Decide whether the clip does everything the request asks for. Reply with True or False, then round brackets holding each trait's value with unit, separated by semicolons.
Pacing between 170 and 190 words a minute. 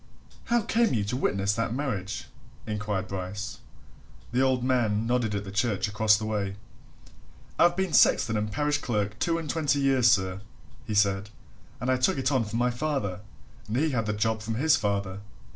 True (185 wpm)